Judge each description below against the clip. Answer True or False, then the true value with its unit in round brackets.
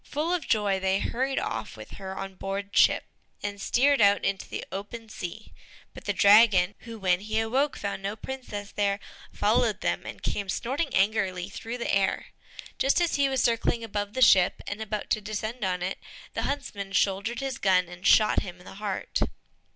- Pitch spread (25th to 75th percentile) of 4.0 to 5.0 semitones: False (3.2 semitones)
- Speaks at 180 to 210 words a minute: True (195 wpm)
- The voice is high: True (205 Hz)